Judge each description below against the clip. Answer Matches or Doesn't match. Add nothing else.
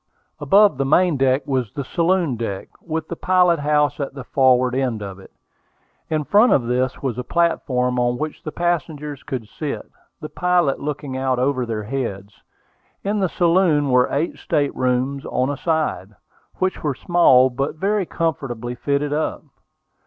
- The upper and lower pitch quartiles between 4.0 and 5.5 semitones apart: Matches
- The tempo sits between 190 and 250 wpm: Doesn't match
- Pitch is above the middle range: Doesn't match